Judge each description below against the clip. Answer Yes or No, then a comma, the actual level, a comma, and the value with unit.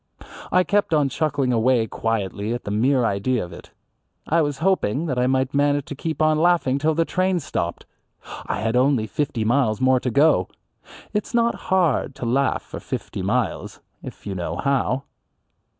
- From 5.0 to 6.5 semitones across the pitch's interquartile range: Yes, average, 5.3 semitones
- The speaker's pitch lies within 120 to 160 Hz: Yes, low, 135 Hz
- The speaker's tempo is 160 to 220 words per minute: Yes, average, 180 wpm